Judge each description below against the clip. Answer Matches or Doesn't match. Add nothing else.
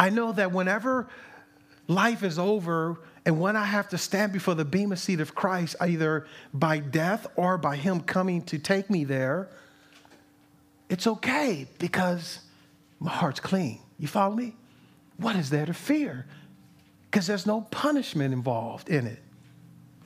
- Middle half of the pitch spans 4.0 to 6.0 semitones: Matches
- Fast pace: Doesn't match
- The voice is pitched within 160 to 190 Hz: Matches